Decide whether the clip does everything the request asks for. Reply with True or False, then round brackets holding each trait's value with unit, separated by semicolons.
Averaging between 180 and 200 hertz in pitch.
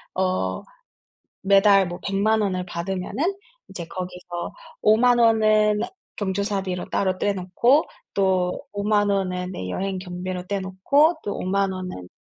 True (190 Hz)